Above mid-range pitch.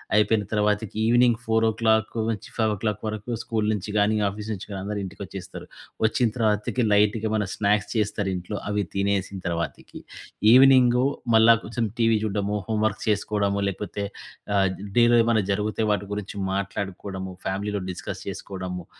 No: low, 105 Hz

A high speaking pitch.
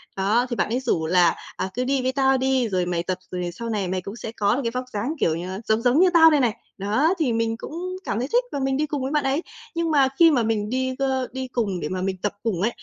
Yes: high, 240 Hz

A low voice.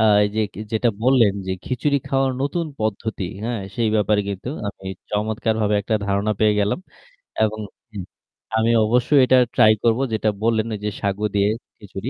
Yes: low, 110 Hz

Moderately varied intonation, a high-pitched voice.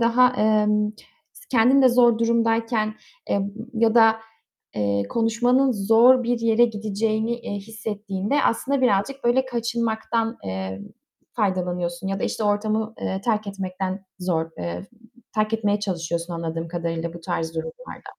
Yes: average, 3.8 semitones; high, 215 Hz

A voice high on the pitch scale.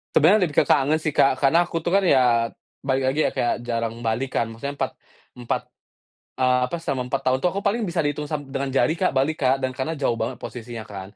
No: low, 135 Hz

